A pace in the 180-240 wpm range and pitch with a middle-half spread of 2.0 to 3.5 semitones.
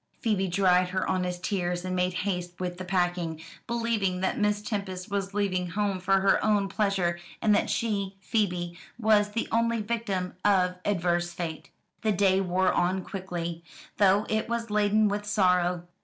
No: average, 165 wpm; narrow, 2.5 semitones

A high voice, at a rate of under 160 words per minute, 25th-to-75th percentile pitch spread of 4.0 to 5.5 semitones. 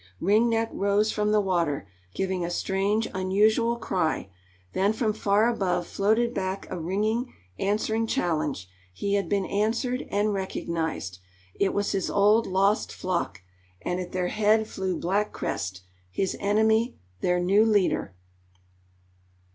No: high, 200 Hz; average, 140 wpm; average, 3.0 semitones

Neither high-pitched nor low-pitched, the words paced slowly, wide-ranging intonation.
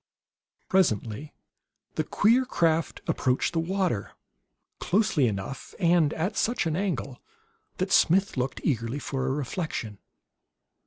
Yes: medium, 155 Hz; slow, 115 wpm; wide, 6.4 semitones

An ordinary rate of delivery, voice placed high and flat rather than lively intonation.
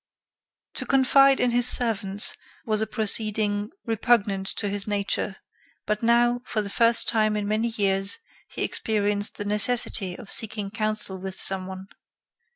Yes: average, 150 wpm; high, 210 Hz; narrow, 2.3 semitones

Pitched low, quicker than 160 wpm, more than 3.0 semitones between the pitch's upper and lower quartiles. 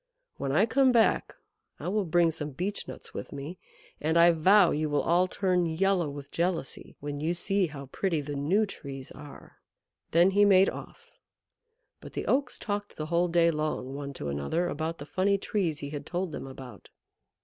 No: medium, 170 Hz; average, 190 wpm; average, 4.7 semitones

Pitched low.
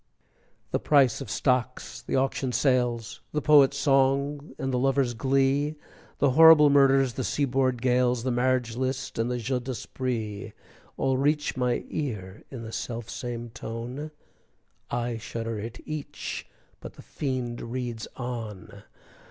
Yes: low, 125 Hz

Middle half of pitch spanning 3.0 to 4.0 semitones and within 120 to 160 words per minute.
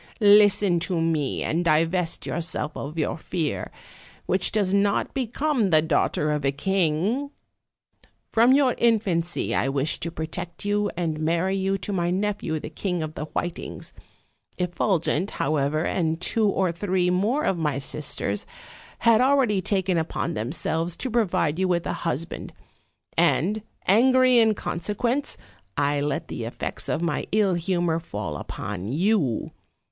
No: average, 4.7 semitones; average, 150 wpm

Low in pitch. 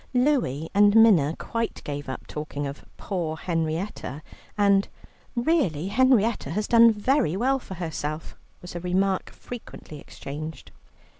No: high, 190 Hz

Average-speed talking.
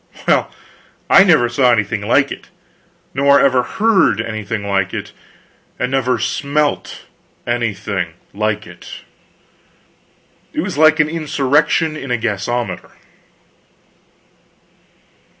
No: slow, 105 wpm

